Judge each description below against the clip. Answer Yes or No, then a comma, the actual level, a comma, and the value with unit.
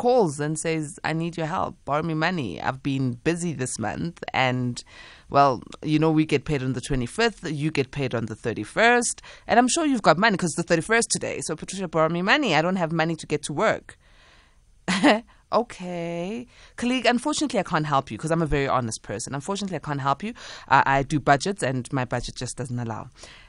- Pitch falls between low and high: Yes, medium, 155 Hz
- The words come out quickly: Yes, fast, 210 wpm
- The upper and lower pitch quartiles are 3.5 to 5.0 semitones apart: No, wide, 5.4 semitones